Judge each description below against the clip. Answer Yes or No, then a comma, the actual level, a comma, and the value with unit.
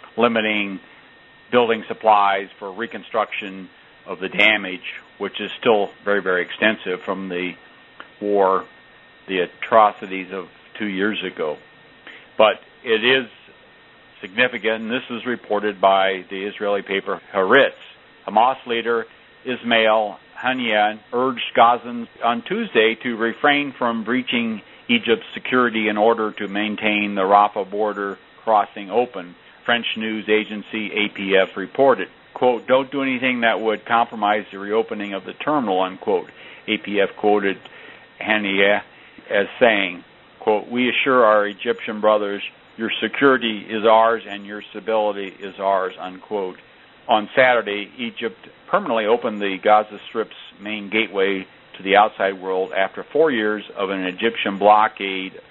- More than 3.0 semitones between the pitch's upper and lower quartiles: No, average, 2.7 semitones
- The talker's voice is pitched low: Yes, low, 105 Hz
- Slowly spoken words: Yes, slow, 130 wpm